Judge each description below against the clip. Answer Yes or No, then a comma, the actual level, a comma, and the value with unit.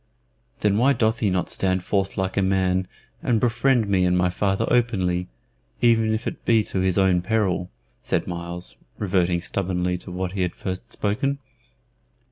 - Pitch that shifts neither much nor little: Yes, average, 3.4 semitones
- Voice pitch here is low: Yes, very low, 95 Hz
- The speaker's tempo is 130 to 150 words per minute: No, average, 170 wpm